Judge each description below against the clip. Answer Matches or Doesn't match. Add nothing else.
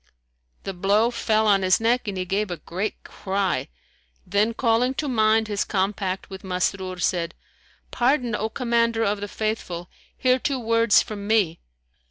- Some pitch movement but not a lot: Matches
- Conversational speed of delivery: Matches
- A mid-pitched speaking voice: Doesn't match